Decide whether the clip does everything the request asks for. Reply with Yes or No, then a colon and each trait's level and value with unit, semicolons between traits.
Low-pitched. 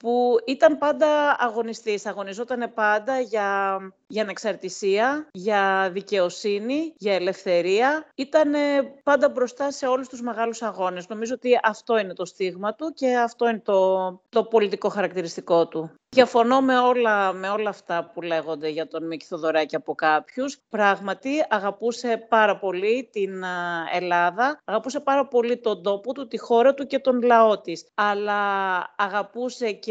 No: high, 215 Hz